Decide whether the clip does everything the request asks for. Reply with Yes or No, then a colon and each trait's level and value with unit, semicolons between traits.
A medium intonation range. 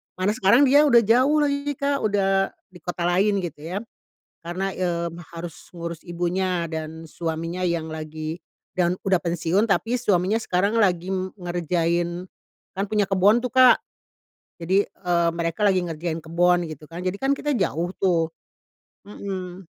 Yes: average, 3.0 semitones